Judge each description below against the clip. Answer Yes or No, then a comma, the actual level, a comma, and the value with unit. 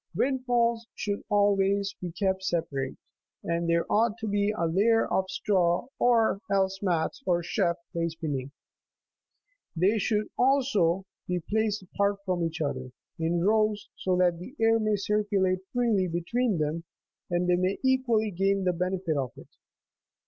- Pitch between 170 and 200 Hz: Yes, high, 190 Hz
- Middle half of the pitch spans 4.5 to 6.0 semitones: No, average, 3.8 semitones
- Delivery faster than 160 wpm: No, average, 155 wpm